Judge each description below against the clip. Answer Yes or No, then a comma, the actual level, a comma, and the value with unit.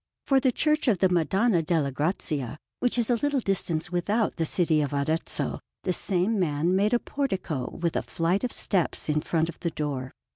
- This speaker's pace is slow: No, average, 195 wpm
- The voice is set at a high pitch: No, medium, 175 Hz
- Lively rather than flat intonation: Yes, wide, 5.7 semitones